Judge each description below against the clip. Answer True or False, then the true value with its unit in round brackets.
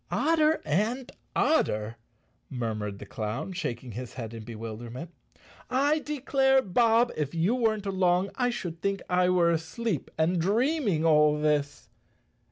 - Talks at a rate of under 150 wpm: True (140 wpm)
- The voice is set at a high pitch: False (175 Hz)